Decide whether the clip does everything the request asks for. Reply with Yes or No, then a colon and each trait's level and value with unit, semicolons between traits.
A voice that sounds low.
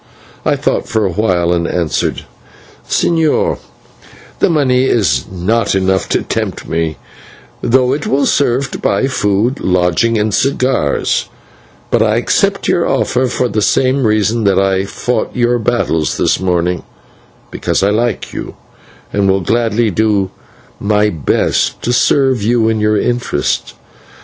Yes: low, 110 Hz